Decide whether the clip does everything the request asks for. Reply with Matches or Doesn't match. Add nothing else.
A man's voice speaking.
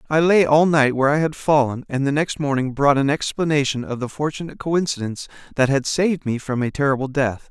Matches